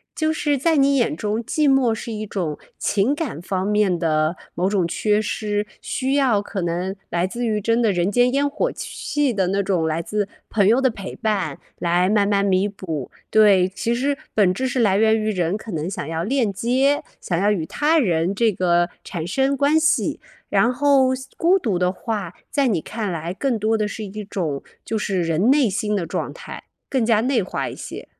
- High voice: Yes, high, 210 Hz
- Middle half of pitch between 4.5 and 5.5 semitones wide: Yes, average, 5.2 semitones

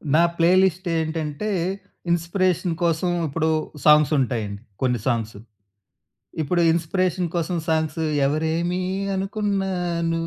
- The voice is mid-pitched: Yes, medium, 165 Hz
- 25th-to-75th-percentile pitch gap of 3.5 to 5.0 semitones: No, average, 3.0 semitones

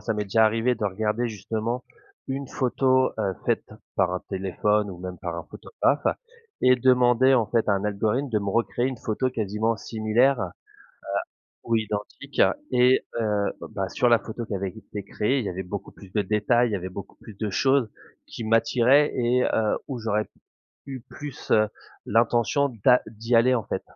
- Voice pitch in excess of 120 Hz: No, low, 110 Hz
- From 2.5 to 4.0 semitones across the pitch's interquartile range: Yes, average, 3.3 semitones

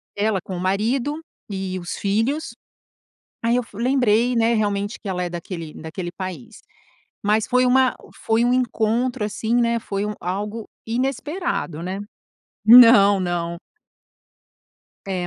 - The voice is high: Yes, high, 215 Hz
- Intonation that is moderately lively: Yes, average, 4.3 semitones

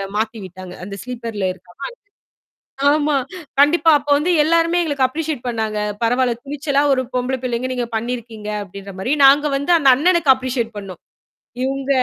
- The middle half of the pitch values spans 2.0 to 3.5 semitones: No, average, 4.6 semitones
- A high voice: Yes, very high, 255 Hz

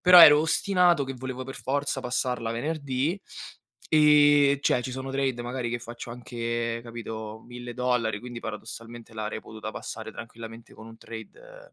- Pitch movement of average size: Yes, average, 3.5 semitones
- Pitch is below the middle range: Yes, low, 125 Hz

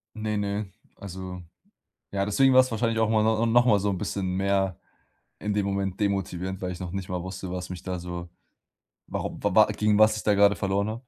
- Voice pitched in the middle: No, low, 100 Hz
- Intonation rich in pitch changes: No, narrow, 2.5 semitones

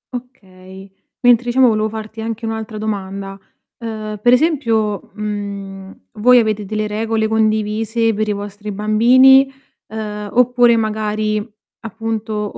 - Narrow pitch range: Yes, narrow, 1.5 semitones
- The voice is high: Yes, high, 215 Hz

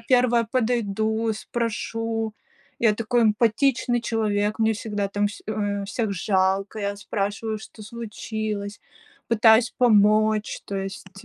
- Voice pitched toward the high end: Yes, high, 215 Hz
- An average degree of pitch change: No, narrow, 1.9 semitones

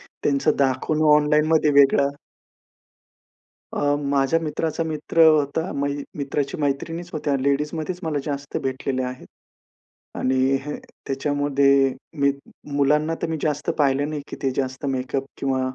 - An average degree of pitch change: No, narrow, 1.9 semitones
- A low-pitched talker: No, medium, 145 Hz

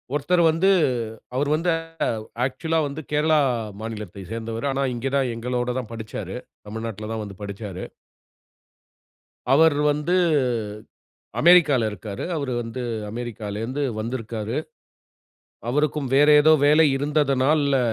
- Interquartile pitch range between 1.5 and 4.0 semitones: No, average, 4.8 semitones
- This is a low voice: Yes, low, 130 Hz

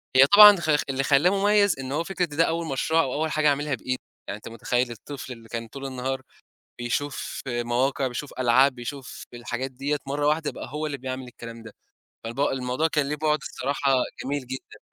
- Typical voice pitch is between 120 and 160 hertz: Yes, low, 135 Hz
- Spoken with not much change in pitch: No, average, 3.1 semitones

